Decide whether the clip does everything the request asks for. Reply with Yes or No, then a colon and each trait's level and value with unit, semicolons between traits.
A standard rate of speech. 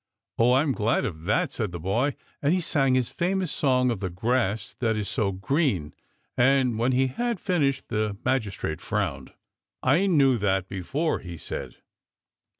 Yes: average, 175 wpm